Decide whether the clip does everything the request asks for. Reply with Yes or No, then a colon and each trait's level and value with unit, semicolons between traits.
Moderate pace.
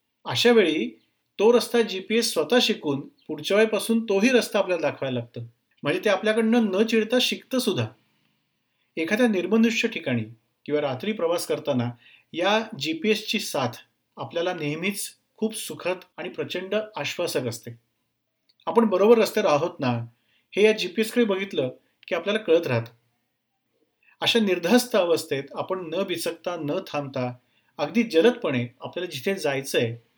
No: fast, 140 wpm